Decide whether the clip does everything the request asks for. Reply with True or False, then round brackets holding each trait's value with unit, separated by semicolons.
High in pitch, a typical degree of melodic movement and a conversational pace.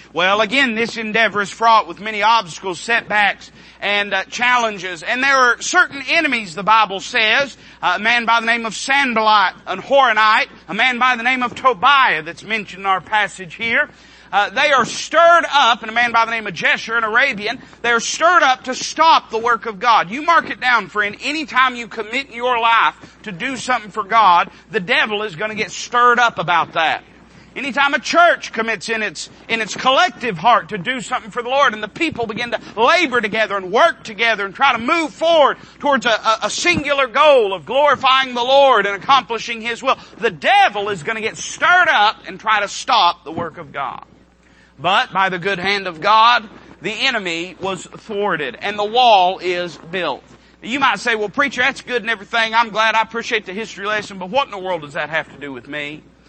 False (230 Hz; 4.1 semitones; 210 wpm)